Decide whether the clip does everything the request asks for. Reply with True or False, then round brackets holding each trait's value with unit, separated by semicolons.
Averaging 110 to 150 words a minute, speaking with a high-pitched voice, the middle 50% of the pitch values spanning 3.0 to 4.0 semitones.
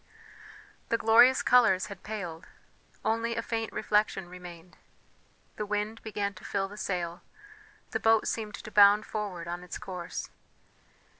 True (140 wpm; 205 Hz; 3.5 semitones)